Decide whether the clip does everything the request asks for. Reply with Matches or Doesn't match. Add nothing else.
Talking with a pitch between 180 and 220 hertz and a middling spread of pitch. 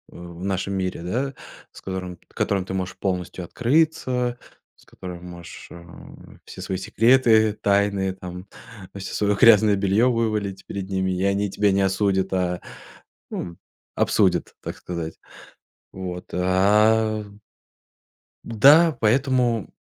Doesn't match